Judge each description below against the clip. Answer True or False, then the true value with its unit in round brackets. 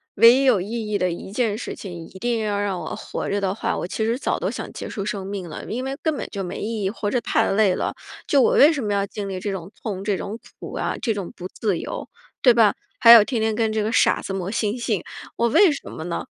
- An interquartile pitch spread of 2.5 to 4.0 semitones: True (3.0 semitones)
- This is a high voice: True (210 Hz)